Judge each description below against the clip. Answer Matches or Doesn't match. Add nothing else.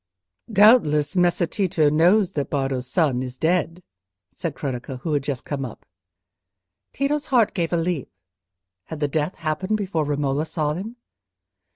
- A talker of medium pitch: Matches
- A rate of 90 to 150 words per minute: Matches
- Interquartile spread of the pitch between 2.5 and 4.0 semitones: Doesn't match